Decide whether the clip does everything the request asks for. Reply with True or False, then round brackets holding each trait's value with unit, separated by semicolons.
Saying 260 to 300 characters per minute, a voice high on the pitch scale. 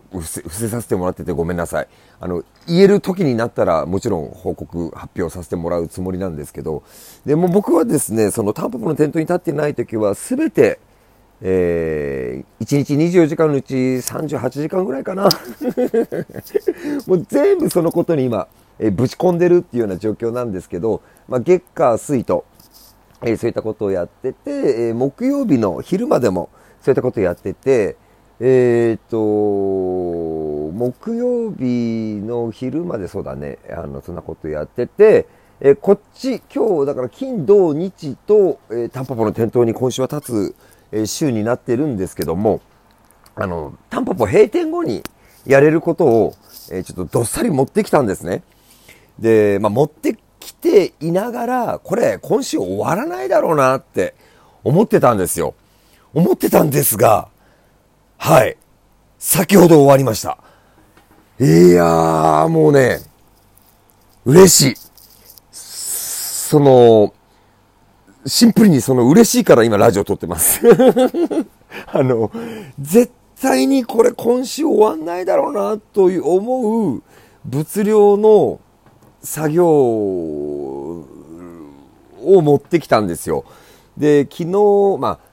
False (280 characters per minute; 135 Hz)